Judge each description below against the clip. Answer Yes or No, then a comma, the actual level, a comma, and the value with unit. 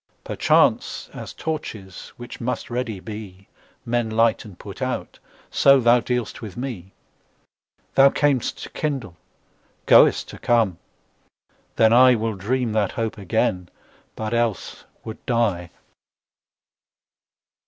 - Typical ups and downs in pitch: Yes, average, 3.1 semitones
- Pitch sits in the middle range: No, low, 115 Hz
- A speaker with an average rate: No, slow, 110 wpm